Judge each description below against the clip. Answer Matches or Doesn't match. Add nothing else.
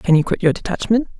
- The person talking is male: Doesn't match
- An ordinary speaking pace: Doesn't match